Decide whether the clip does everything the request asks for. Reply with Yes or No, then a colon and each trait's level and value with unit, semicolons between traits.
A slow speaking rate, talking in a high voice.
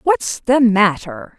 Yes: slow, 130 wpm; high, 225 Hz